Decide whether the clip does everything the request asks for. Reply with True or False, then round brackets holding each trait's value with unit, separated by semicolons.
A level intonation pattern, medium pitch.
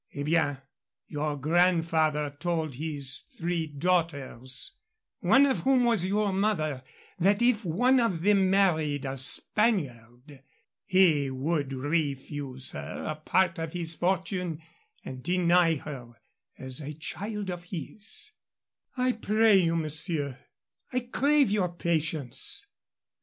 False (5.0 semitones; 165 Hz)